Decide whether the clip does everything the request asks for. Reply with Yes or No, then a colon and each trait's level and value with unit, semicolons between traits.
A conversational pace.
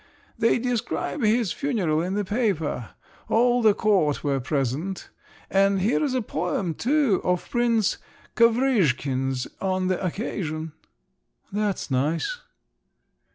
No: slow, 110 wpm